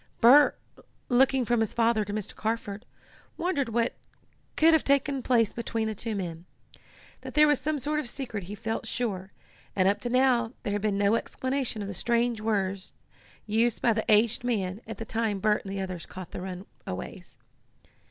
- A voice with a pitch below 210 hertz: No, high, 225 Hz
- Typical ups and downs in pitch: Yes, average, 3.4 semitones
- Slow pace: No, average, 190 wpm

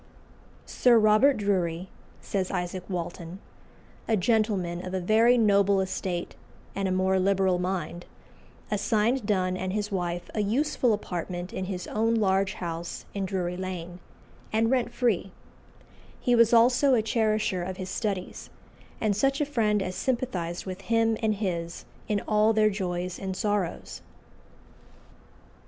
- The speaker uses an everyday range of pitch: Yes, average, 3.2 semitones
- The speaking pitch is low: No, high, 195 Hz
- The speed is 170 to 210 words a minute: No, average, 145 wpm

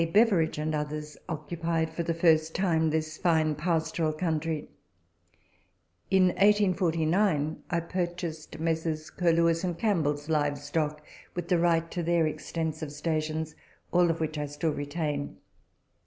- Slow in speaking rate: Yes, slow, 125 wpm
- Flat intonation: Yes, narrow, 1.8 semitones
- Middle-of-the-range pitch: Yes, medium, 160 Hz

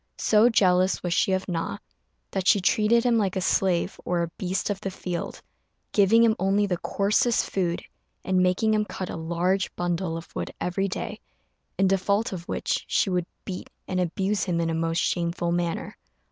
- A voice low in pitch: No, medium, 185 Hz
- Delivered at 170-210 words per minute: Yes, average, 190 wpm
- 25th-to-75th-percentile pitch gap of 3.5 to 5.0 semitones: No, narrow, 2.5 semitones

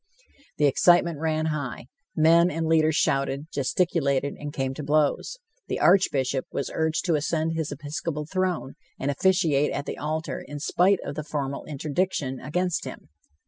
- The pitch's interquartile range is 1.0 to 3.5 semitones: Yes, average, 2.7 semitones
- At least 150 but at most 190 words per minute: Yes, average, 155 wpm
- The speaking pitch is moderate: Yes, medium, 155 Hz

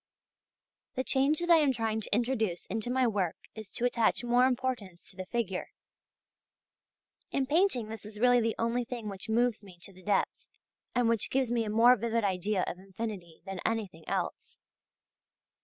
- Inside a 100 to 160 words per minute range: No, average, 175 wpm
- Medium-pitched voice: No, high, 225 Hz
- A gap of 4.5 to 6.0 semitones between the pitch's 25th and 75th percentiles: No, average, 3.6 semitones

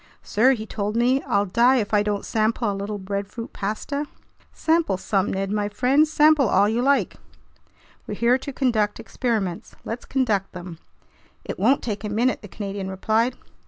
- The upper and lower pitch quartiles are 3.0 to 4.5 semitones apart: Yes, average, 4.0 semitones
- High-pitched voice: Yes, high, 215 Hz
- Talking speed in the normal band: Yes, average, 170 wpm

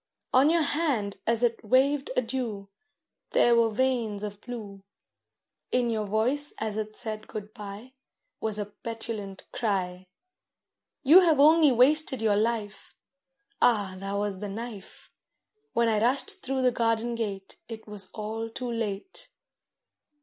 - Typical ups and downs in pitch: Yes, average, 3.5 semitones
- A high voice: Yes, high, 225 Hz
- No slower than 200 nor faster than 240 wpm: No, average, 140 wpm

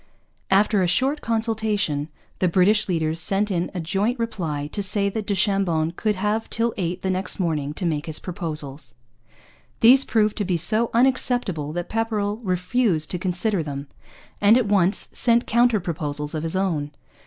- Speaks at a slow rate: No, average, 170 wpm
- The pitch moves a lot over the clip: No, average, 4.8 semitones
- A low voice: No, high, 190 Hz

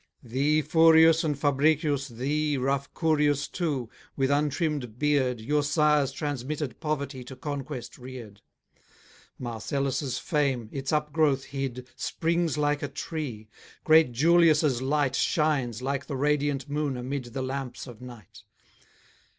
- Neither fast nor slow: No, slow, 125 wpm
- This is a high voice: No, medium, 140 Hz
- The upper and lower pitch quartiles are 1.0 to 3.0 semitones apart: Yes, average, 2.7 semitones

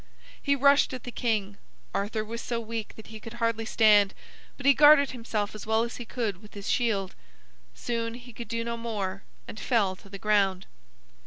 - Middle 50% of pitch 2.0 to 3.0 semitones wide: Yes, narrow, 2.4 semitones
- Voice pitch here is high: Yes, high, 225 Hz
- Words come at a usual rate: Yes, average, 195 wpm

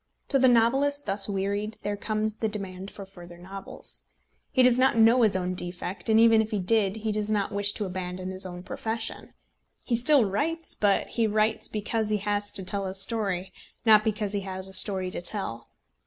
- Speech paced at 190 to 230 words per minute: Yes, average, 200 wpm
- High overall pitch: Yes, high, 205 Hz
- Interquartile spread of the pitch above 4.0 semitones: No, average, 2.7 semitones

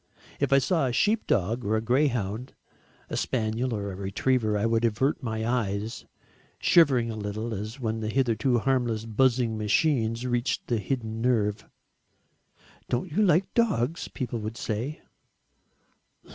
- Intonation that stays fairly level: No, average, 3.1 semitones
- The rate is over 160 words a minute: No, average, 145 wpm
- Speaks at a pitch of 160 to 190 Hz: No, low, 115 Hz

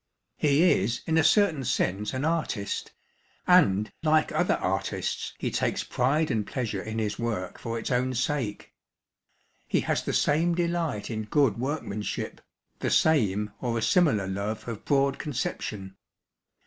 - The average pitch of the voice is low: Yes, low, 125 Hz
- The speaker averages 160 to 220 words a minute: No, average, 150 wpm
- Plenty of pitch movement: Yes, wide, 6.5 semitones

